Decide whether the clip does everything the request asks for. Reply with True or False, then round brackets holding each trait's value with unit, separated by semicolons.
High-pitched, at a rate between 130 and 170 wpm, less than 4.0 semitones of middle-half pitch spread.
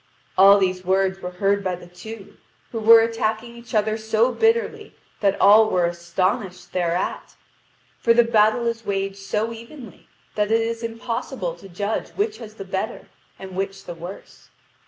True (210 Hz; 165 wpm; 3.3 semitones)